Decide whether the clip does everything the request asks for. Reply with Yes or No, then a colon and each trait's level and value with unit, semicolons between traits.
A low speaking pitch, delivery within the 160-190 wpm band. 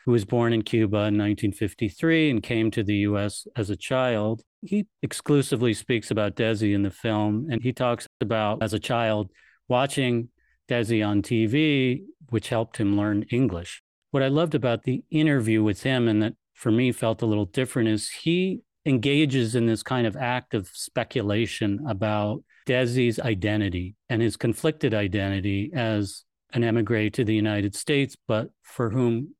Yes: low, 115 Hz; average, 165 wpm